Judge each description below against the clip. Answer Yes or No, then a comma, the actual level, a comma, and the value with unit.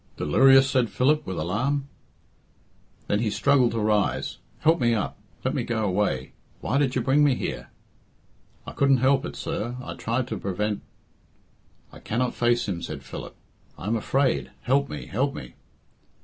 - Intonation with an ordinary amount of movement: Yes, average, 4.6 semitones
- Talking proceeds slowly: No, average, 170 wpm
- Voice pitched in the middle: No, low, 125 Hz